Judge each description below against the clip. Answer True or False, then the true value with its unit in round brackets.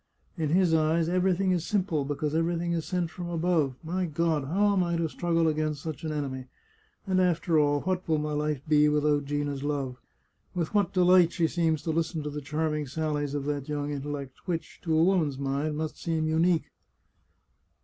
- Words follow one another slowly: False (195 wpm)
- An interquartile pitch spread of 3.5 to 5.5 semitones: False (2.8 semitones)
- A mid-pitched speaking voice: True (160 Hz)